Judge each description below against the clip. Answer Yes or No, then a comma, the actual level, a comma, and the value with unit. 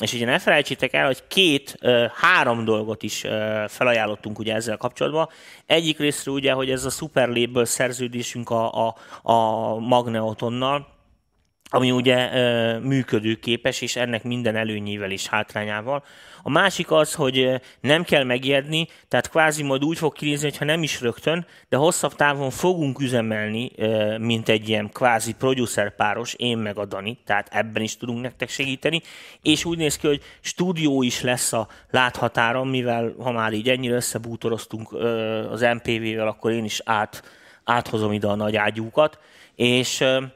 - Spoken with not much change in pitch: No, average, 3.6 semitones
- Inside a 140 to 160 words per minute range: Yes, average, 150 wpm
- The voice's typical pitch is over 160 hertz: No, low, 120 Hz